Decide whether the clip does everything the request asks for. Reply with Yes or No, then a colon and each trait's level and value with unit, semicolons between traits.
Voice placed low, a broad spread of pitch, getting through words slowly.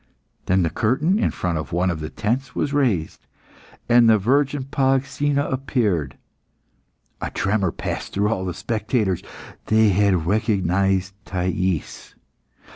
Yes: low, 105 Hz; wide, 6.0 semitones; slow, 130 wpm